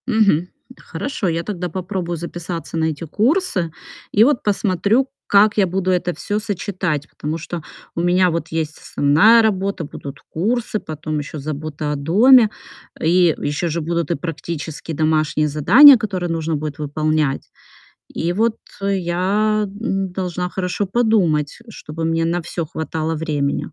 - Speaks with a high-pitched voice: No, medium, 170 Hz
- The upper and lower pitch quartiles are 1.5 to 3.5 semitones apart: No, average, 4.2 semitones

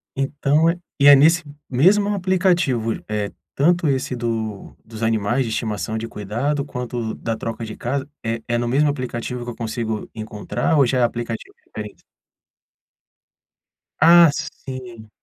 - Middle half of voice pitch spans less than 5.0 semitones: Yes, average, 4.2 semitones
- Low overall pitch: Yes, low, 120 Hz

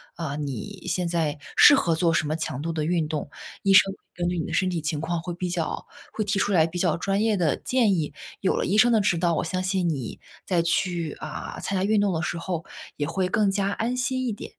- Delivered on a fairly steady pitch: No, average, 3.3 semitones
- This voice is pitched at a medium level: Yes, medium, 175 Hz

